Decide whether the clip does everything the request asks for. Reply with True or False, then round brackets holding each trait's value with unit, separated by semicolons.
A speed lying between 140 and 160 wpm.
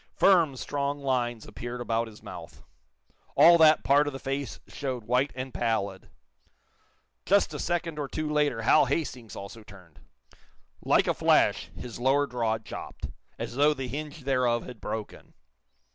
True (155 wpm)